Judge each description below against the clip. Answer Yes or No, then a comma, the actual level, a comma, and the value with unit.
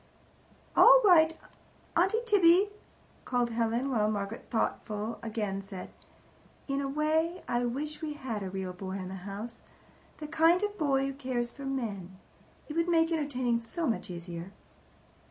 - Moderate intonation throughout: No, wide, 7.2 semitones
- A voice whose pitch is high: Yes, very high, 255 Hz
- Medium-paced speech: Yes, average, 155 wpm